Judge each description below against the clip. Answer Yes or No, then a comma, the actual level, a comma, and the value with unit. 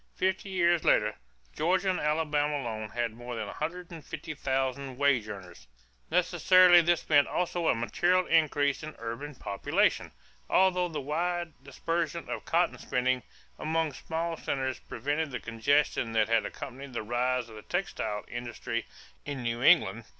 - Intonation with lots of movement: Yes, wide, 5.9 semitones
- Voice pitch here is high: No, medium, 140 Hz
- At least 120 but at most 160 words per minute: Yes, average, 155 wpm